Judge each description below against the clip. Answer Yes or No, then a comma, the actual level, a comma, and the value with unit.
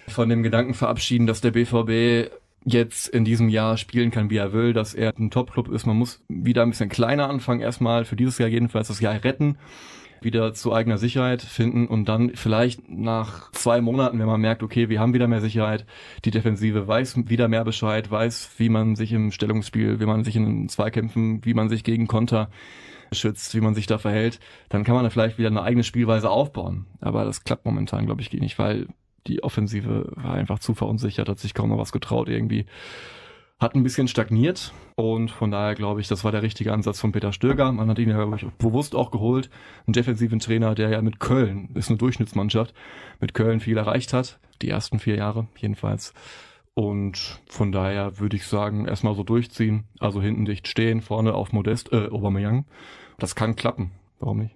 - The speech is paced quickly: Yes, fast, 200 wpm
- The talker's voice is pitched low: Yes, low, 115 Hz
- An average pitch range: No, narrow, 1.7 semitones